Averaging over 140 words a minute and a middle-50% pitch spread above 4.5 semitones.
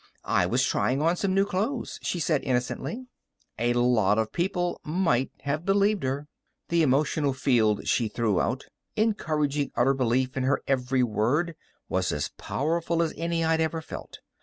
Yes: average, 160 wpm; average, 5.3 semitones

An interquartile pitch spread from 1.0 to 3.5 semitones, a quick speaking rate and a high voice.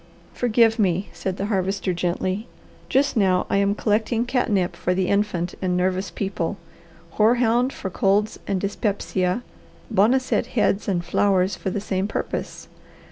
No: average, 2.9 semitones; average, 140 wpm; high, 200 Hz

